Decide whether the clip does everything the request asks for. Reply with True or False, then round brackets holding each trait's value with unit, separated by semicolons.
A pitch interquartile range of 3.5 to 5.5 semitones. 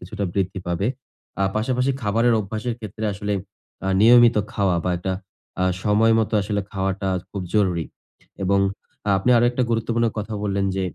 False (2.8 semitones)